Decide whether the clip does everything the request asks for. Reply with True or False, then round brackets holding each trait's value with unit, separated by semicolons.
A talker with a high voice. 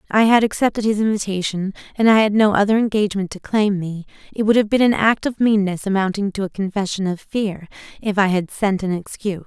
True (205 Hz)